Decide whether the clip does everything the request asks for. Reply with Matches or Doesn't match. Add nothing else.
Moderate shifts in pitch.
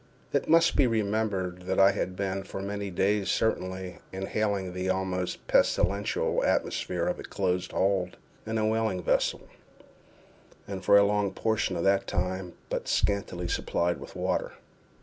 Doesn't match